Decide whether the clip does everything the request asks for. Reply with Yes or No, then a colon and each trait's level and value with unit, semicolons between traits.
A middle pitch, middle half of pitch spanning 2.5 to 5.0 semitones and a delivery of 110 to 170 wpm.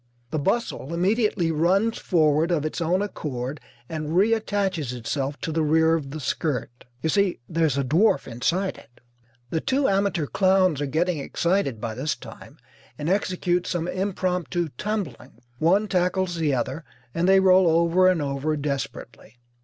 Yes: medium, 165 Hz; average, 4.2 semitones; average, 160 wpm